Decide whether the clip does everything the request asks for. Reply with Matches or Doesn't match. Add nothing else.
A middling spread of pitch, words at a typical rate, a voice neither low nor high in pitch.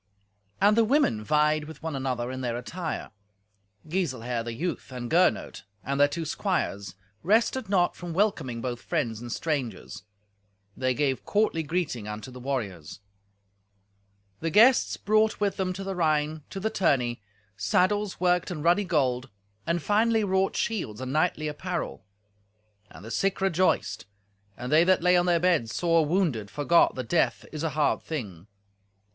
Doesn't match